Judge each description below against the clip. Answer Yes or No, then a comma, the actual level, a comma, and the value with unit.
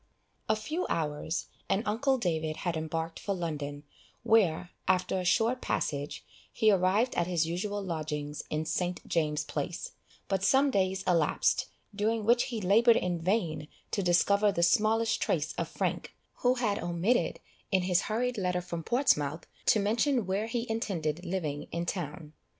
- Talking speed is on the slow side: No, average, 155 wpm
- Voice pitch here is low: No, medium, 185 Hz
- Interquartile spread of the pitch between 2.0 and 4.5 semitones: No, average, 5.0 semitones